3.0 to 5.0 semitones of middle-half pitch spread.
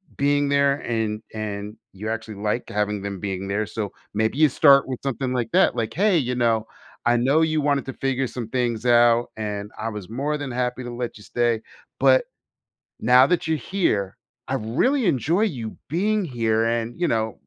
Yes: average, 4.4 semitones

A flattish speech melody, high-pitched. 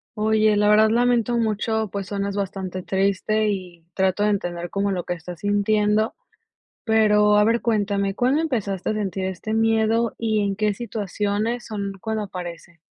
Yes: narrow, 2.0 semitones; high, 210 Hz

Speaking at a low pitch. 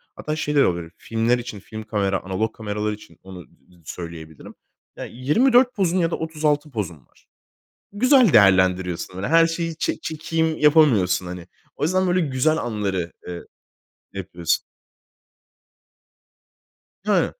Yes: low, 115 Hz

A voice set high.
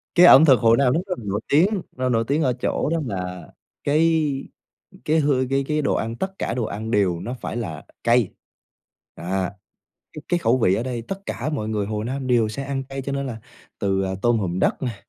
No: low, 125 Hz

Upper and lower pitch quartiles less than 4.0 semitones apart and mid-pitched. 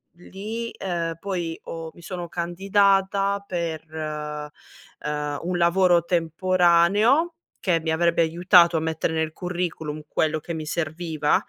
Yes: narrow, 2.5 semitones; medium, 170 Hz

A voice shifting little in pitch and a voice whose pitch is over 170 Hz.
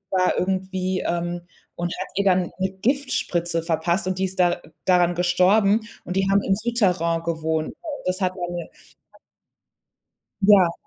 Yes: narrow, 1.9 semitones; medium, 185 Hz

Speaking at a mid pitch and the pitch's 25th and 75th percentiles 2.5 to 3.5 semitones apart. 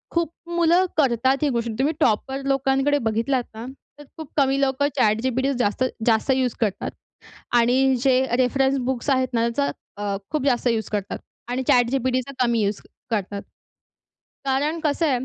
No: very high, 260 Hz; average, 2.9 semitones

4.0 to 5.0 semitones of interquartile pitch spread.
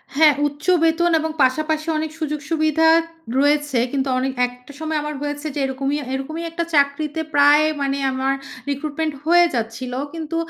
No: narrow, 2.4 semitones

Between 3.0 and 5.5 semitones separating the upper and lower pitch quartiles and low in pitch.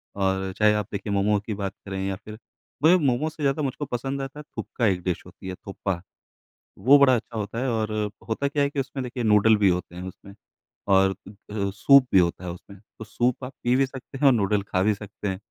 Yes: average, 5.2 semitones; low, 105 Hz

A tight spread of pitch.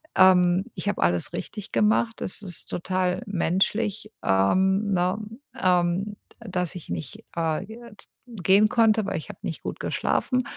No: average, 3.0 semitones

